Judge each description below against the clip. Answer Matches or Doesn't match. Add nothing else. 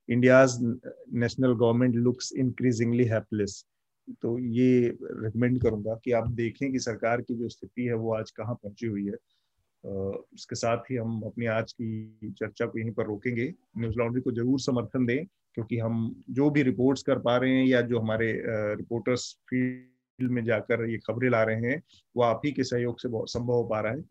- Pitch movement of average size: Doesn't match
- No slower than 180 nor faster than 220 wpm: Matches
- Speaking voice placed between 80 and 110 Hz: Doesn't match